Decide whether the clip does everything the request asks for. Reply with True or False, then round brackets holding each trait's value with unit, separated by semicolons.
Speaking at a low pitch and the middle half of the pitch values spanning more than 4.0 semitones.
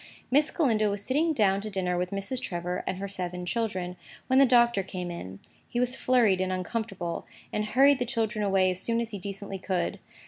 False (200 Hz; 4.4 semitones)